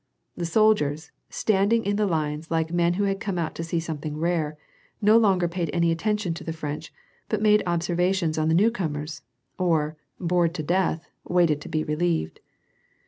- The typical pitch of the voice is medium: Yes, medium, 170 Hz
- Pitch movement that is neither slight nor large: Yes, average, 3.4 semitones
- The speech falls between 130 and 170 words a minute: No, average, 180 wpm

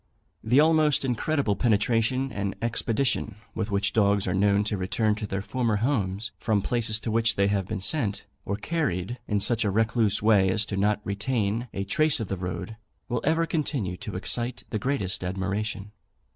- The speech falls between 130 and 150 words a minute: No, average, 180 wpm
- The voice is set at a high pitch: No, low, 110 Hz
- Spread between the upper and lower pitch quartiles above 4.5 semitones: No, average, 3.4 semitones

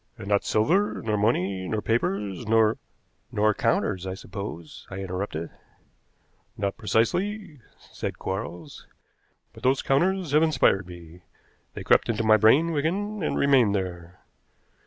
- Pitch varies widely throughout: Yes, wide, 6.6 semitones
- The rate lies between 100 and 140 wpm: Yes, slow, 135 wpm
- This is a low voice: Yes, low, 110 Hz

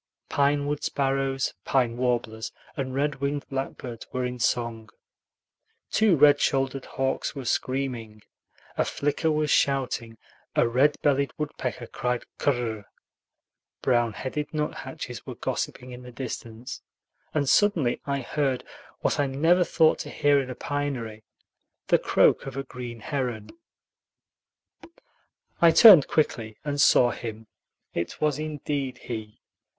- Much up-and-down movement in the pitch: No, average, 3.1 semitones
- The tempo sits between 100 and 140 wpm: Yes, slow, 135 wpm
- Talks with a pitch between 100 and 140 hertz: Yes, low, 135 Hz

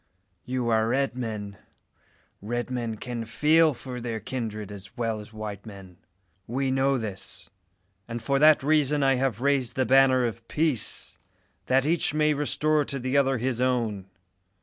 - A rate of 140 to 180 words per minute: Yes, average, 160 wpm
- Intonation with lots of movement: No, average, 3.5 semitones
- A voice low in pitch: Yes, low, 125 Hz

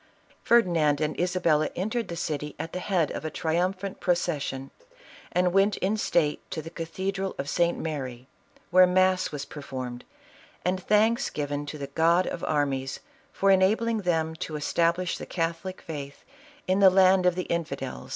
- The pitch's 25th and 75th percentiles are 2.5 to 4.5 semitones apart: Yes, average, 4.0 semitones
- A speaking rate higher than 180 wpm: No, average, 160 wpm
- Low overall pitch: No, medium, 170 Hz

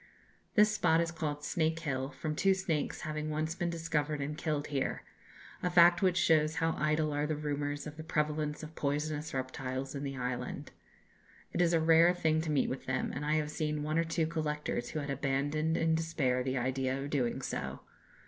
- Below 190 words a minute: No, average, 200 wpm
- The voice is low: No, medium, 150 Hz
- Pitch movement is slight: Yes, narrow, 2.1 semitones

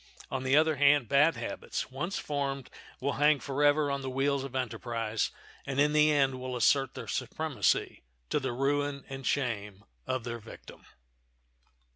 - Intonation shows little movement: Yes, narrow, 2.1 semitones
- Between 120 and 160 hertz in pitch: Yes, low, 135 Hz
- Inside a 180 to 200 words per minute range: No, average, 160 wpm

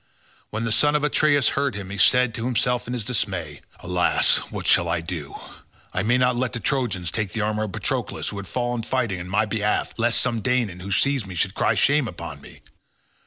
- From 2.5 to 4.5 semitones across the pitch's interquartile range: No, average, 5.0 semitones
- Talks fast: Yes, fast, 215 wpm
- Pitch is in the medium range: No, low, 110 Hz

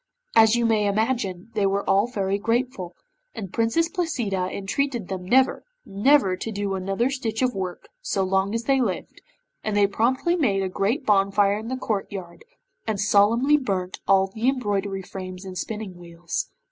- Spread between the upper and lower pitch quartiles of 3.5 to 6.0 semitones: Yes, average, 3.8 semitones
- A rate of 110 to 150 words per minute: No, average, 170 wpm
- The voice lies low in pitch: No, high, 205 Hz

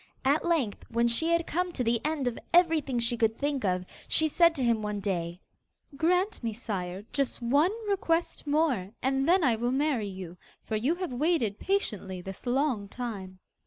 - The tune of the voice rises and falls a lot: Yes, wide, 7.1 semitones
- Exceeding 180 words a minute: Yes, average, 190 wpm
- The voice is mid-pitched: No, very high, 250 Hz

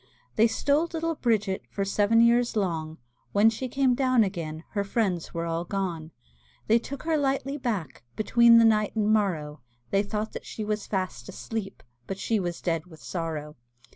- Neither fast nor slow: Yes, average, 175 wpm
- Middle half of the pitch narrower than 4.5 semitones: No, average, 5.2 semitones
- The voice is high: Yes, high, 210 Hz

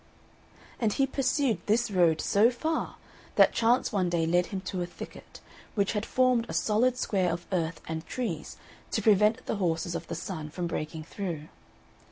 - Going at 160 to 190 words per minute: Yes, average, 180 wpm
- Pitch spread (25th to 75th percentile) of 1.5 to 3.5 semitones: No, average, 5.3 semitones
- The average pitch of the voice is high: Yes, high, 195 Hz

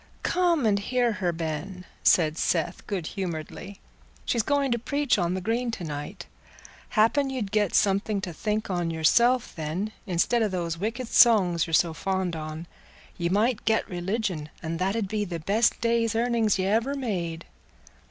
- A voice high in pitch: Yes, high, 200 Hz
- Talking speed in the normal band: Yes, average, 170 wpm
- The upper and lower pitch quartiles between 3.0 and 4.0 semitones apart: No, average, 5.0 semitones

